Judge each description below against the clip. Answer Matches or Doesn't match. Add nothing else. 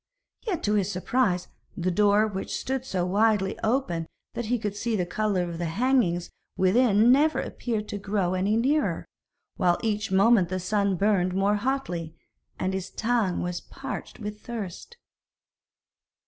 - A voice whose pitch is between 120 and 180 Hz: Doesn't match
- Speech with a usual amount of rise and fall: Matches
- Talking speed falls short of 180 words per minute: Matches